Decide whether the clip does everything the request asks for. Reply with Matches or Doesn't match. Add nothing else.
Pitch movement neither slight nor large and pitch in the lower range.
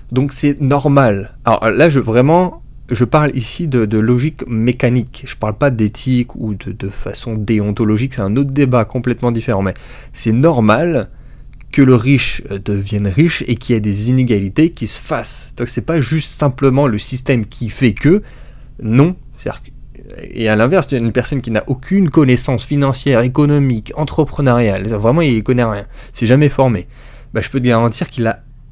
Matches